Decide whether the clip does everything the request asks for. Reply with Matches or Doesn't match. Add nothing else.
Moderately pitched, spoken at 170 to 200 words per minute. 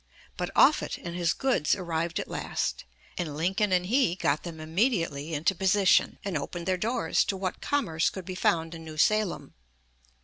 Matches